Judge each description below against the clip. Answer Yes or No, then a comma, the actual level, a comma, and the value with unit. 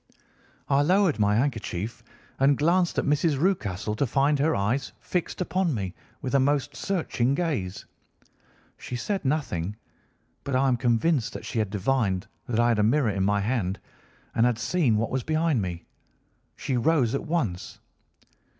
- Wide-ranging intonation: Yes, wide, 5.9 semitones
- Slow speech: No, average, 165 wpm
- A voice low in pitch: Yes, low, 130 Hz